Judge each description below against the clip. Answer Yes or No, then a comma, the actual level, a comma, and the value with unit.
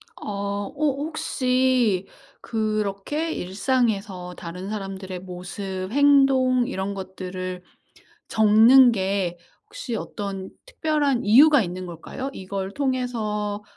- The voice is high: Yes, high, 210 Hz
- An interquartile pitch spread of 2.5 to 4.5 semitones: No, average, 5.3 semitones